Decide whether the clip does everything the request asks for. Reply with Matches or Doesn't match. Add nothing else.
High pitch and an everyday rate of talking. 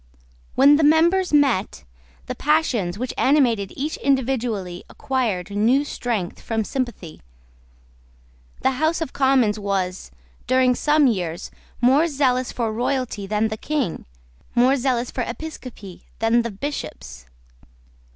Doesn't match